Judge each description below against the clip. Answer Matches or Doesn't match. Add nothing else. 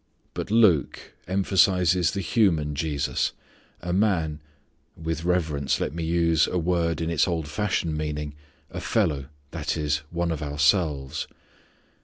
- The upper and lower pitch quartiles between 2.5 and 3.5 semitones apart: Matches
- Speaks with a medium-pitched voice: Doesn't match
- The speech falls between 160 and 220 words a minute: Doesn't match